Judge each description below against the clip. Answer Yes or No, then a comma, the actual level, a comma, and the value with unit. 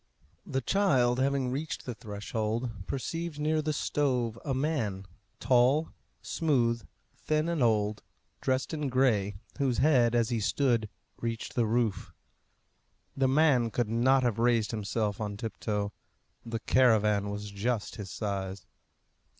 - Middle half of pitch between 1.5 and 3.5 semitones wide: No, average, 4.0 semitones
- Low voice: Yes, low, 120 Hz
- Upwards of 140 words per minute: No, slow, 135 wpm